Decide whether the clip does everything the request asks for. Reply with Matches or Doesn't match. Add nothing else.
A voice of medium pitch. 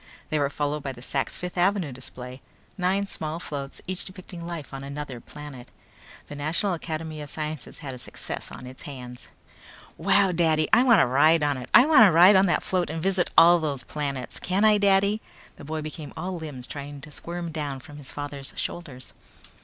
Matches